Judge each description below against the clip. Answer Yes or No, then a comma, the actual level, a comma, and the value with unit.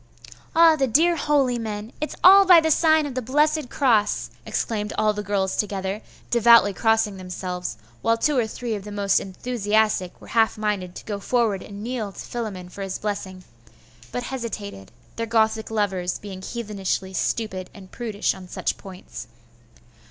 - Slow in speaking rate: No, average, 165 wpm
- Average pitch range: Yes, average, 3.7 semitones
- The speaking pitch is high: Yes, high, 215 Hz